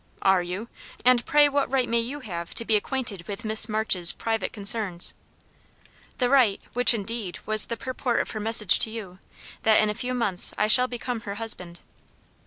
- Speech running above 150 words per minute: Yes, average, 190 wpm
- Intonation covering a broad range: No, average, 3.6 semitones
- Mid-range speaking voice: No, high, 220 Hz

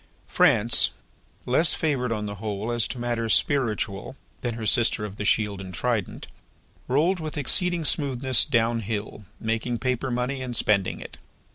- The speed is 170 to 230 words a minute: No, average, 155 wpm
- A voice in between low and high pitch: No, low, 120 Hz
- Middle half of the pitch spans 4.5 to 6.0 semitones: No, average, 3.6 semitones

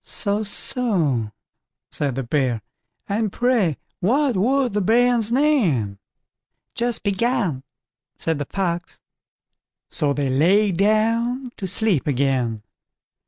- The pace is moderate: No, slow, 110 wpm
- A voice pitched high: Yes, high, 200 Hz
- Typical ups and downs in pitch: No, wide, 8.6 semitones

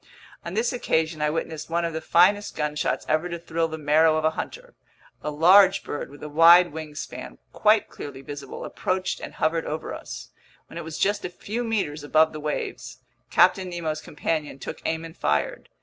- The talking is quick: No, average, 190 wpm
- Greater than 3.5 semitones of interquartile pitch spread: No, average, 2.7 semitones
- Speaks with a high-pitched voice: No, medium, 160 Hz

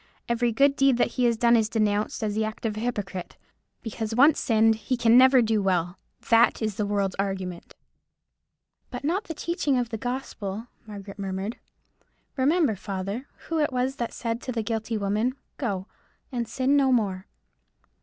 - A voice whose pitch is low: No, high, 225 Hz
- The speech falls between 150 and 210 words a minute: Yes, average, 175 wpm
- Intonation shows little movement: No, average, 3.6 semitones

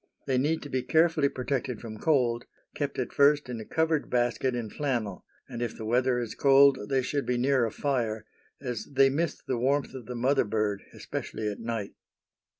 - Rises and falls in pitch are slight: No, average, 3.2 semitones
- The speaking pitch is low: Yes, low, 125 Hz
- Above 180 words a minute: Yes, average, 195 wpm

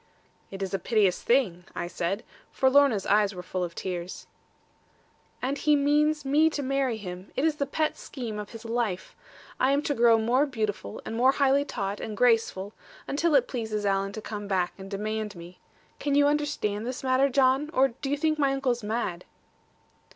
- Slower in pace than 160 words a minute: No, average, 190 wpm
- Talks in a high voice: Yes, high, 235 Hz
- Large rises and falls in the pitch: Yes, wide, 5.8 semitones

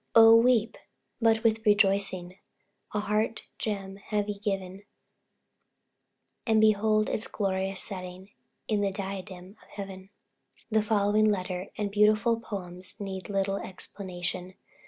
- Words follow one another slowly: Yes, slow, 120 wpm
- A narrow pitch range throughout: Yes, narrow, 2.1 semitones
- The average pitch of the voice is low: No, high, 200 Hz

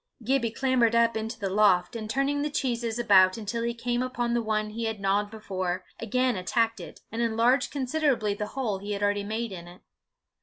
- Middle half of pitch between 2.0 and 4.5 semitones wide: Yes, average, 2.9 semitones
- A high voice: Yes, high, 225 Hz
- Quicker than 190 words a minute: Yes, average, 200 wpm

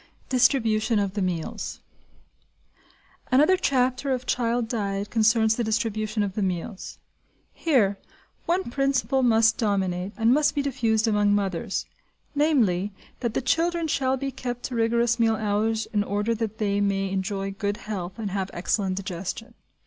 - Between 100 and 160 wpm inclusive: Yes, average, 150 wpm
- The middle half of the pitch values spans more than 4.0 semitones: No, average, 3.7 semitones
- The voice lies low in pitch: No, high, 220 Hz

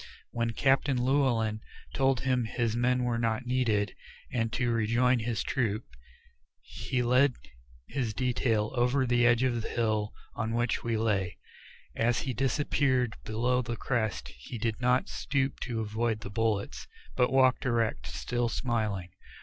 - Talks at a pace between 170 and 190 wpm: No, average, 150 wpm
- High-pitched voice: No, low, 120 Hz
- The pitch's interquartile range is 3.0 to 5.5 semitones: No, narrow, 2.4 semitones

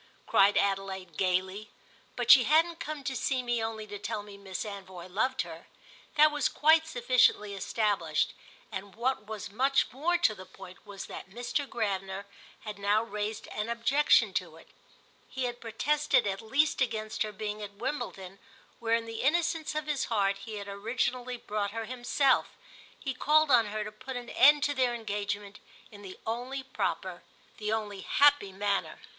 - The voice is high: Yes, high, 220 Hz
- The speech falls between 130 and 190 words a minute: Yes, average, 175 wpm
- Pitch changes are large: No, average, 4.4 semitones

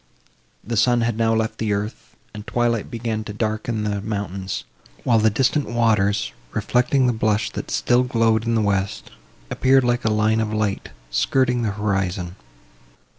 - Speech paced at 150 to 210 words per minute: Yes, average, 165 wpm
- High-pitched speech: No, low, 110 Hz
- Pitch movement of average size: No, narrow, 2.3 semitones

